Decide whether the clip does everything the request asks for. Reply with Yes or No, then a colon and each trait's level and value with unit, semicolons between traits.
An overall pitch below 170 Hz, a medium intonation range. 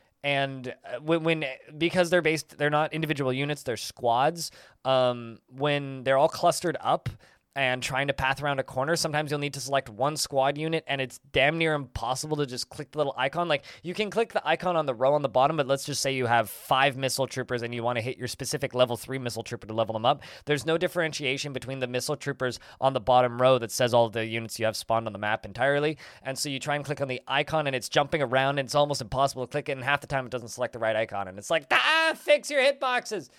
Yes: low, 135 Hz; average, 3.1 semitones